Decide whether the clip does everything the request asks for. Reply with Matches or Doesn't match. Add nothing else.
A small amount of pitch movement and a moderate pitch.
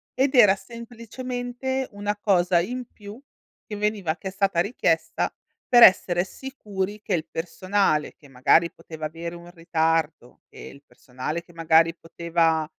Doesn't match